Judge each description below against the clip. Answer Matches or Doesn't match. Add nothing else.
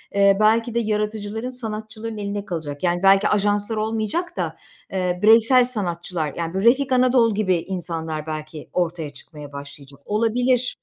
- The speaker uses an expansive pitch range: Doesn't match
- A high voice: Matches